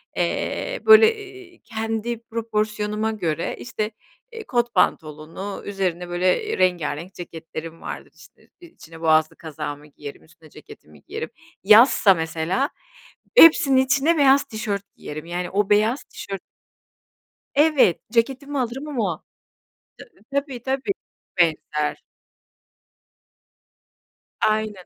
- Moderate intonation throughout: No, wide, 8.0 semitones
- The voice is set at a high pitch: Yes, high, 210 Hz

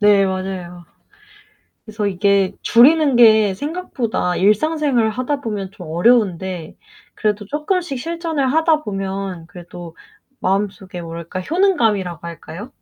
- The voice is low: No, high, 205 Hz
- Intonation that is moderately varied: No, wide, 6.4 semitones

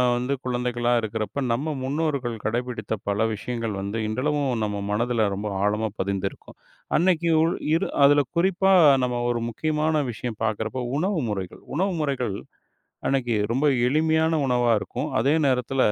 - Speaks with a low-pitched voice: Yes, low, 125 Hz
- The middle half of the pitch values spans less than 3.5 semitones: No, average, 5.3 semitones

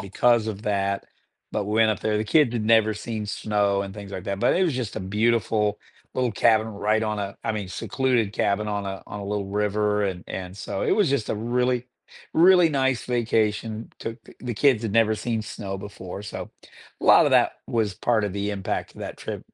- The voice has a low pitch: Yes, low, 105 Hz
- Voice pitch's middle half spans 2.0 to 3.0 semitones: Yes, narrow, 2.5 semitones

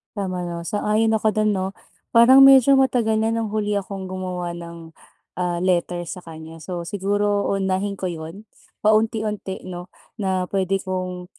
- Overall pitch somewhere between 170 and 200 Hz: Yes, high, 190 Hz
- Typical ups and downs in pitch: Yes, average, 3.2 semitones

